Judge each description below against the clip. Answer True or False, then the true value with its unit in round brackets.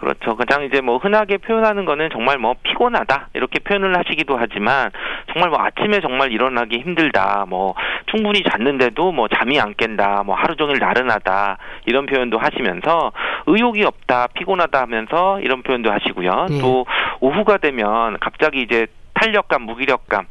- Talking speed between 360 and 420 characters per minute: True (365 characters per minute)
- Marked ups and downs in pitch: True (7.6 semitones)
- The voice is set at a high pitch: False (130 Hz)